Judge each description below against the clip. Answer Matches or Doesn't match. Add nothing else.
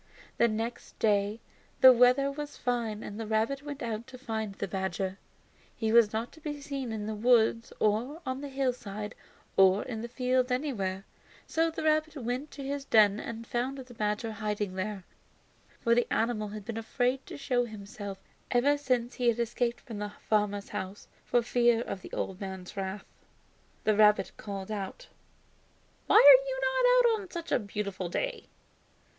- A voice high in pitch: Matches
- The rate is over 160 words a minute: Matches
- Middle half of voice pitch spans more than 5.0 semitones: Doesn't match